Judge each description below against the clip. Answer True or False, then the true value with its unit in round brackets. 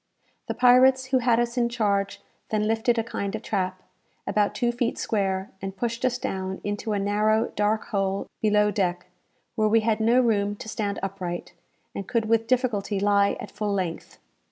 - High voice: True (210 Hz)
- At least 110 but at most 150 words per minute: False (180 wpm)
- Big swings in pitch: False (2.7 semitones)